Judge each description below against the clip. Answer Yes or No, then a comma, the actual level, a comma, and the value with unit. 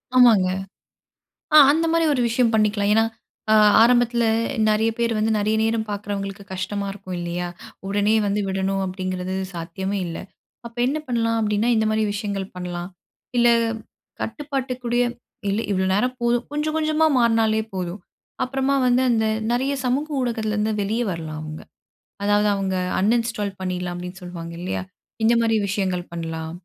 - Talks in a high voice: Yes, high, 210 Hz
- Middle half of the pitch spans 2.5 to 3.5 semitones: No, average, 4.0 semitones